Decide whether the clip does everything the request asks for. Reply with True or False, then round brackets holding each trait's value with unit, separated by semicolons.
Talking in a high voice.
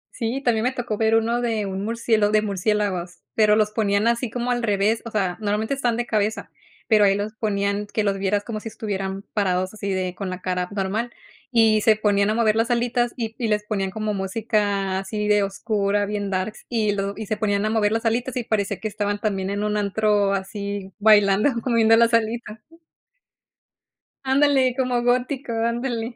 True (215 Hz)